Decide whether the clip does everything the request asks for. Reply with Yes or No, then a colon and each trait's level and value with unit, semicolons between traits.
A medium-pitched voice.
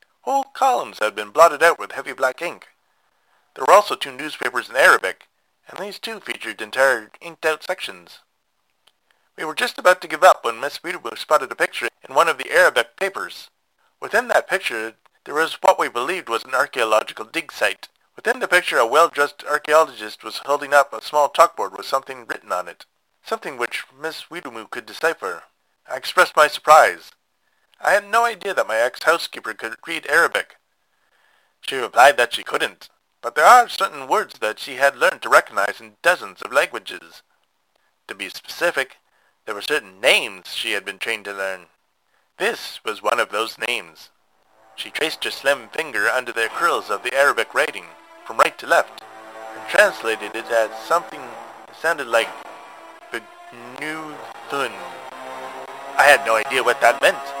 Yes: medium, 145 Hz